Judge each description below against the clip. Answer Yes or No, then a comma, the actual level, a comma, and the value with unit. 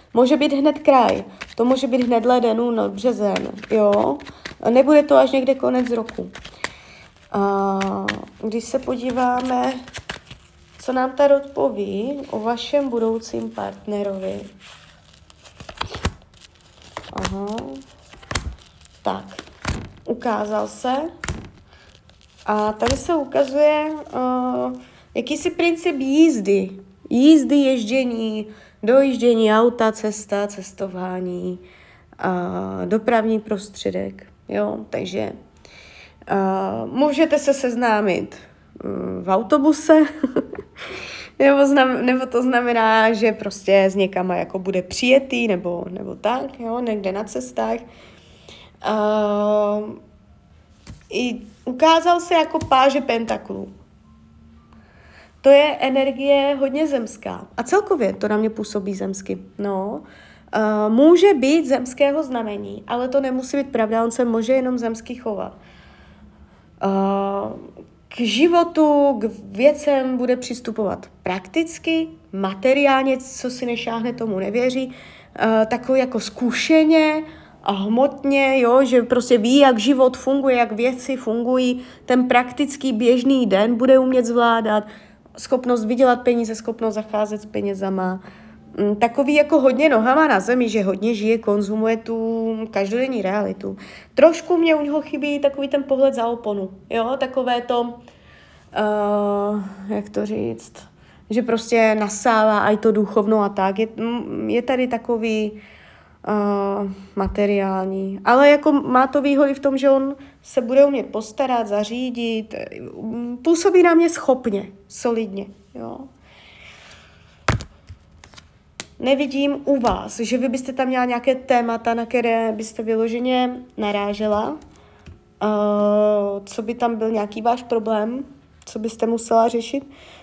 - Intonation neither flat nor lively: Yes, average, 4.8 semitones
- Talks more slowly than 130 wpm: Yes, slow, 115 wpm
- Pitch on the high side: Yes, high, 230 Hz